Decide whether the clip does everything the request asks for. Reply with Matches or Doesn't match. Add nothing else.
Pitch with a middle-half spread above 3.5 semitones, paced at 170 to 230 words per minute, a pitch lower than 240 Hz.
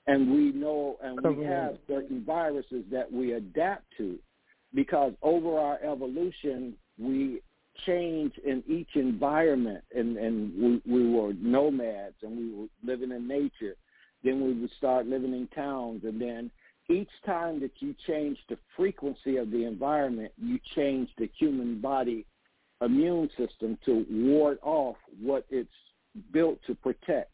Doesn't match